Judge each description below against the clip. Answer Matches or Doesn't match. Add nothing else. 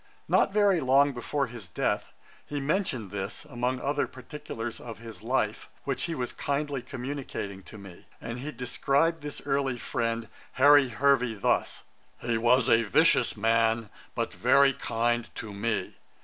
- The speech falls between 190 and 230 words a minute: Doesn't match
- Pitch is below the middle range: Matches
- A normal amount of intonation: Matches